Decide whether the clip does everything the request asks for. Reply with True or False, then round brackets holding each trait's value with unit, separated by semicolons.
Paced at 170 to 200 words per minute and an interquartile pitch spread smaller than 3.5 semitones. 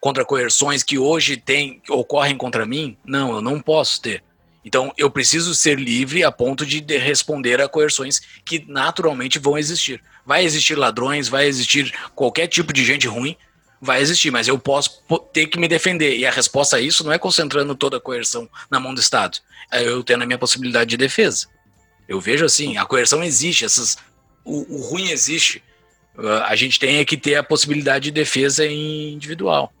True (185 wpm; 2.8 semitones)